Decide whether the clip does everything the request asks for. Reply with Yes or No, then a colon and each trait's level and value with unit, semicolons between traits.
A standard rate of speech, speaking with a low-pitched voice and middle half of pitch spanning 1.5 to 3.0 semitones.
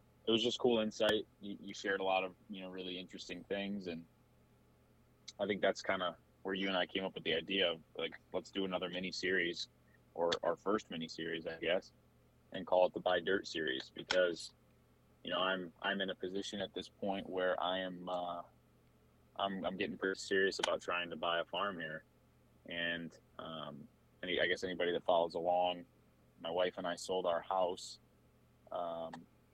Yes: average, 195 wpm; very low, 90 Hz; narrow, 2.5 semitones